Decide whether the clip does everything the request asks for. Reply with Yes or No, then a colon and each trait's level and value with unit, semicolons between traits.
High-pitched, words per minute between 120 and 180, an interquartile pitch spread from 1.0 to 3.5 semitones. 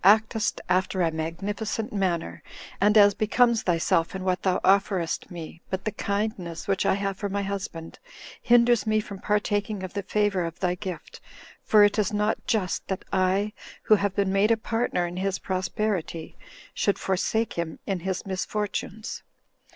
Yes: high, 195 Hz; average, 165 wpm; narrow, 2.4 semitones